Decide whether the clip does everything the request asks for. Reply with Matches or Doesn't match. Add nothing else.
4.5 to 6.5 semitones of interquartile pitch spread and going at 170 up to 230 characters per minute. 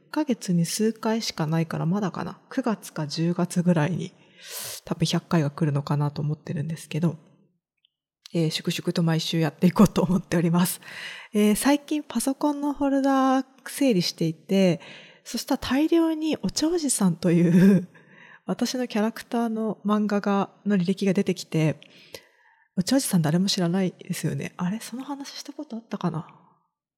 Doesn't match